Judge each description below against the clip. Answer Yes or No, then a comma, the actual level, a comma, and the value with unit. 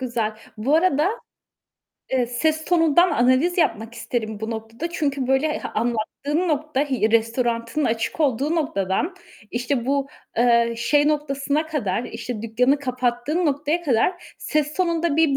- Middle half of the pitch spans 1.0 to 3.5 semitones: No, average, 4.7 semitones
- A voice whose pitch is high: Yes, very high, 270 Hz